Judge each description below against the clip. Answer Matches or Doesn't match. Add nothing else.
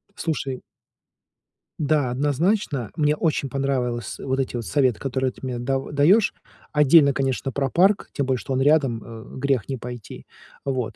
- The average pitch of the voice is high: Doesn't match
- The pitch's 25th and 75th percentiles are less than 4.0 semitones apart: Matches